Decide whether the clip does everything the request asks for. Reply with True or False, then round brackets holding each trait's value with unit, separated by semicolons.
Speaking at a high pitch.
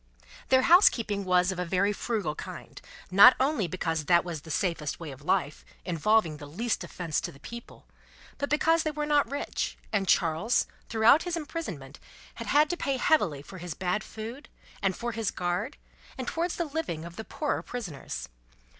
True (205 Hz)